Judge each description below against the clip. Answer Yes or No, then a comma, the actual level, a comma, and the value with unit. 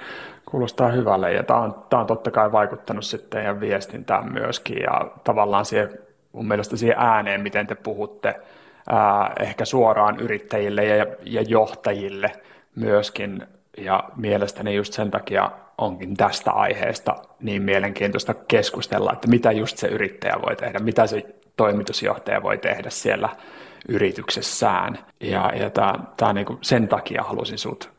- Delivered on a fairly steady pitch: Yes, narrow, 1.1 semitones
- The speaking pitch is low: Yes, low, 105 Hz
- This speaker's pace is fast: No, average, 140 wpm